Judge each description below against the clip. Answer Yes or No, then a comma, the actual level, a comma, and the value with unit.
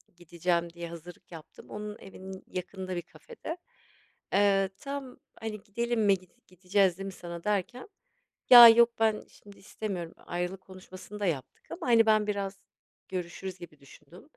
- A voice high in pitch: Yes, high, 195 Hz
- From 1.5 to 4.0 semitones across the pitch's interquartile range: Yes, average, 3.1 semitones